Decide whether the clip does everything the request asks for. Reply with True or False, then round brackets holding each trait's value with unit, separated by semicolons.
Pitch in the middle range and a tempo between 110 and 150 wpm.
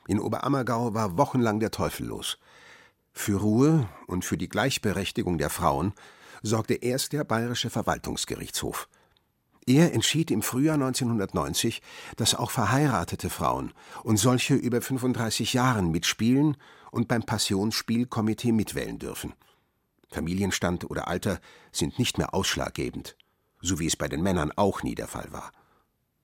False (115 Hz; 135 wpm)